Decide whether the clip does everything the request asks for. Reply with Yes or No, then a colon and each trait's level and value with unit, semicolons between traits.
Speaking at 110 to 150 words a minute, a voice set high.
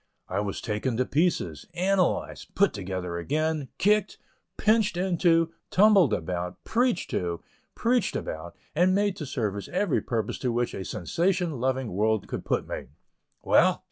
No: average, 145 wpm; medium, 140 Hz